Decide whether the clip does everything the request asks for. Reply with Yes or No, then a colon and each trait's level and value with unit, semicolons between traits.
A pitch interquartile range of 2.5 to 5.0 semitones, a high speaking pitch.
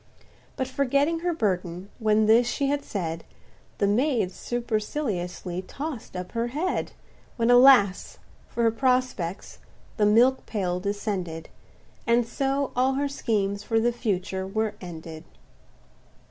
No: wide, 5.4 semitones; high, 225 Hz